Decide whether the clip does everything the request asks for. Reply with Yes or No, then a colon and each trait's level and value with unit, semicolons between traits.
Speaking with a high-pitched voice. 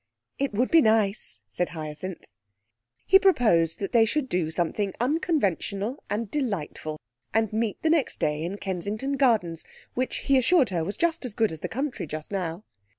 Yes: high, 210 Hz